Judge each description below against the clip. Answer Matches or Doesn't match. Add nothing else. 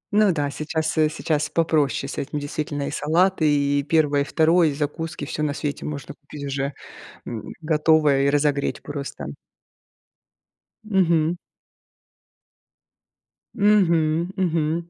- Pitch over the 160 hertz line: Doesn't match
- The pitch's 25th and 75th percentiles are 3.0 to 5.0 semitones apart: Doesn't match